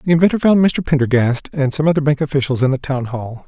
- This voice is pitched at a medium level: Yes, medium, 145 Hz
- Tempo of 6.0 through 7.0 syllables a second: Yes, 6.3 syllables/s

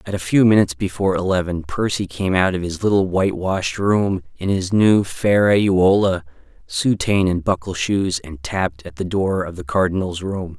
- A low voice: Yes, very low, 95 Hz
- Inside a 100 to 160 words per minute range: No, average, 180 wpm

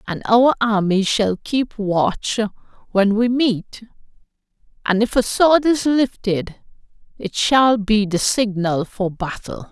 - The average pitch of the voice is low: No, high, 215 Hz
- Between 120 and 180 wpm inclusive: Yes, slow, 135 wpm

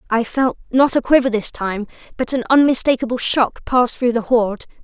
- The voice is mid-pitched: No, high, 245 Hz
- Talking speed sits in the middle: Yes, average, 185 wpm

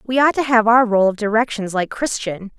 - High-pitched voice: Yes, high, 225 Hz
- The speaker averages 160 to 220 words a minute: No, fast, 230 wpm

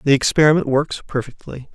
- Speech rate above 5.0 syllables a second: Yes, 5.9 syllables/s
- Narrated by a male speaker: Yes, male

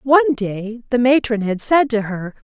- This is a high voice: Yes, high, 235 Hz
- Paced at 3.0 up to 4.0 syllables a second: No, 4.5 syllables/s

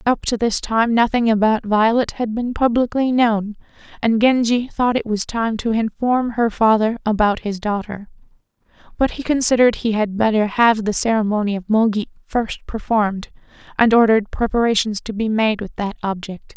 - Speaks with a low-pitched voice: No, high, 220 Hz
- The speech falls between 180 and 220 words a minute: No, average, 165 wpm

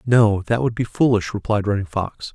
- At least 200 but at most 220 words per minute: Yes, fast, 205 wpm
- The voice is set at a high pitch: No, low, 110 Hz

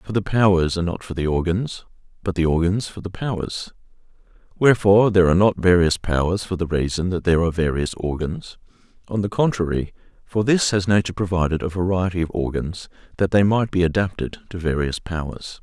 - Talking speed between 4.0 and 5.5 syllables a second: No, 5.9 syllables/s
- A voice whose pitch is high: No, very low, 90 Hz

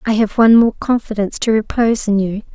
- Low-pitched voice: No, high, 215 Hz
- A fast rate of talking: Yes, fast, 210 wpm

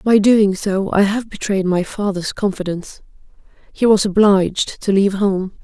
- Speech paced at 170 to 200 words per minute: No, average, 150 wpm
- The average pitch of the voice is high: Yes, high, 200 Hz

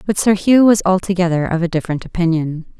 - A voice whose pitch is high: No, medium, 180 Hz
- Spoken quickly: No, average, 195 wpm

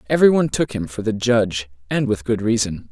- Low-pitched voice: Yes, low, 110 Hz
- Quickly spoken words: Yes, fast, 225 wpm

